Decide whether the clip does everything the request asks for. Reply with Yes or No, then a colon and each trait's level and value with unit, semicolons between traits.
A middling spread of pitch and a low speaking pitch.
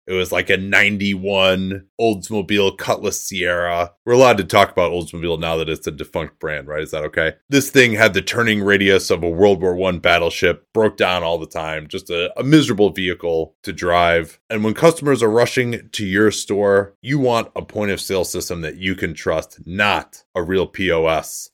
Yes: average, 3.9 semitones; very low, 95 Hz